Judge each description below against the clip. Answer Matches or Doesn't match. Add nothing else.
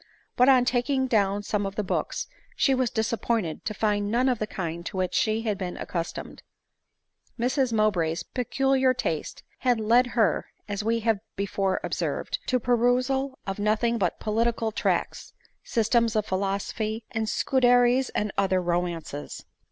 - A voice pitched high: Matches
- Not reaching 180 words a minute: Matches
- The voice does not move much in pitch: Doesn't match